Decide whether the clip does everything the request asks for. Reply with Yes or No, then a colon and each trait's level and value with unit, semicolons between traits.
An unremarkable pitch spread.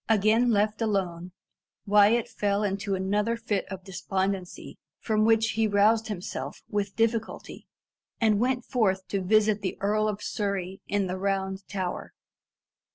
No: narrow, 2.2 semitones